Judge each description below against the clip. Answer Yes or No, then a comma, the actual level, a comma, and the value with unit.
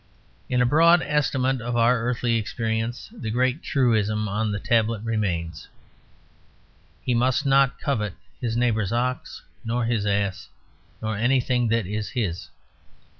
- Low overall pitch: Yes, low, 115 Hz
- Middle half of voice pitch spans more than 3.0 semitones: No, average, 2.7 semitones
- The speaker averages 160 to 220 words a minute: No, slow, 135 wpm